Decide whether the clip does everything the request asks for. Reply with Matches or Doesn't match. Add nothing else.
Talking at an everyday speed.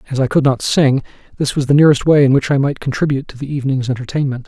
Doesn't match